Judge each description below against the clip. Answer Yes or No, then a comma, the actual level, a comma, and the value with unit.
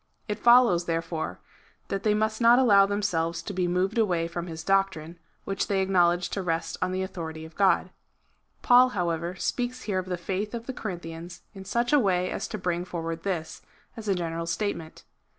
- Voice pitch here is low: No, medium, 185 Hz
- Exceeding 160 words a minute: Yes, average, 190 wpm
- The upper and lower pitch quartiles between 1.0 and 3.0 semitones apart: No, average, 3.6 semitones